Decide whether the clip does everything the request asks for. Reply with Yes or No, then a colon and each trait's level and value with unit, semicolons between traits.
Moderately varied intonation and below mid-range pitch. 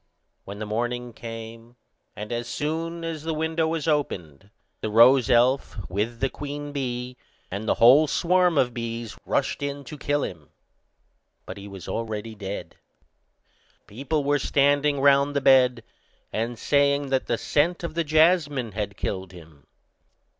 Yes: average, 4.5 semitones; low, 130 Hz